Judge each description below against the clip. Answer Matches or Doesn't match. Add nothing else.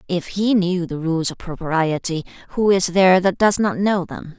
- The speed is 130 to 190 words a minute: Doesn't match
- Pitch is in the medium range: Matches